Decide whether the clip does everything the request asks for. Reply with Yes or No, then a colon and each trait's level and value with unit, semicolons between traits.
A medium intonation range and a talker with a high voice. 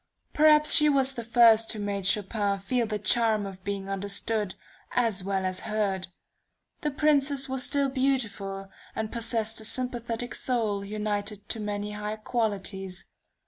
Yes: average, 3.5 semitones; high, 215 Hz